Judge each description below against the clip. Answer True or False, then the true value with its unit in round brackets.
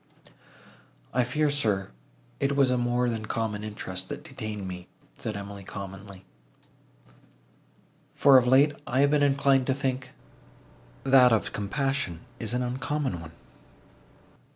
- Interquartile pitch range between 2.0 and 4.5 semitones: False (5.1 semitones)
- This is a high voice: False (120 Hz)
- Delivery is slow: True (130 wpm)